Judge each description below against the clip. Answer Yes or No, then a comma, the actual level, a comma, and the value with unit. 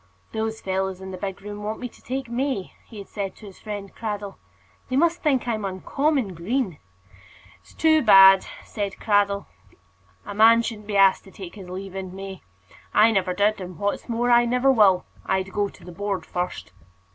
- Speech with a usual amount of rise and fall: Yes, average, 3.2 semitones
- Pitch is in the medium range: No, high, 205 Hz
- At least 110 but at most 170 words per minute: No, average, 195 wpm